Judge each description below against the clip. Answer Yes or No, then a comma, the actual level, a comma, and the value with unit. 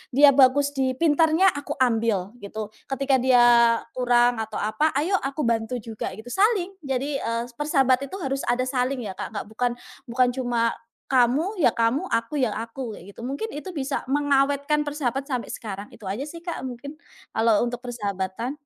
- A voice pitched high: Yes, very high, 255 Hz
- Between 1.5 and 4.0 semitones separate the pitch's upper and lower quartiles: Yes, average, 3.7 semitones